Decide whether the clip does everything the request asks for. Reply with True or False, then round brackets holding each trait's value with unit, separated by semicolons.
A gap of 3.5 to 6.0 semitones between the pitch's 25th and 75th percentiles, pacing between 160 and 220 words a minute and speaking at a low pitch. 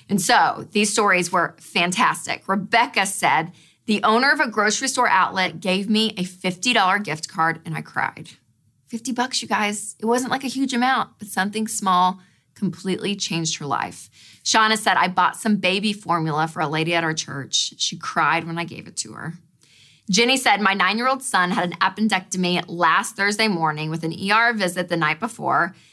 False (4.8 semitones; 185 wpm; 185 Hz)